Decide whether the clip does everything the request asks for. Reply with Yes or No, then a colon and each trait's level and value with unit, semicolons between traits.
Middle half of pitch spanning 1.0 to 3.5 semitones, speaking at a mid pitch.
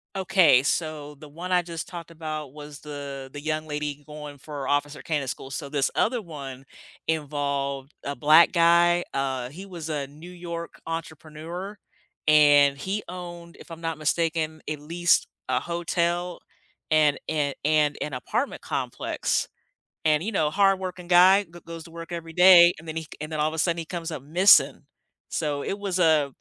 Yes: average, 2.8 semitones; medium, 155 Hz